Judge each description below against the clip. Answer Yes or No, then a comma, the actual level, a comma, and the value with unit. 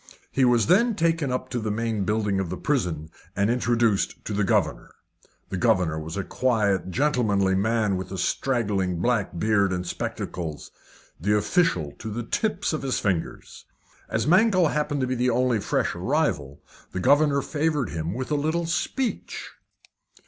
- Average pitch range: No, wide, 6.8 semitones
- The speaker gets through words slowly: No, average, 165 wpm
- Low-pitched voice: Yes, low, 115 Hz